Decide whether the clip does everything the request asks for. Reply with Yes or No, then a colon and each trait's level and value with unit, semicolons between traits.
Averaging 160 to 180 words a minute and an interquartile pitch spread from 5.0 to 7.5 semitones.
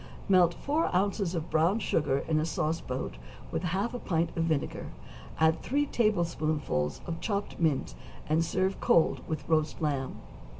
No: average, 165 wpm; average, 3.6 semitones